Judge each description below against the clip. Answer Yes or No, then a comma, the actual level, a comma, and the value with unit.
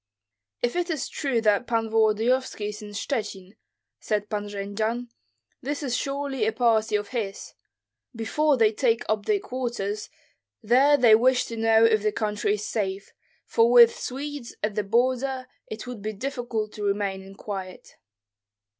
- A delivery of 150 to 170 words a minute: Yes, average, 160 wpm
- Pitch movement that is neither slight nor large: Yes, average, 3.2 semitones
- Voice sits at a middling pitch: No, high, 225 Hz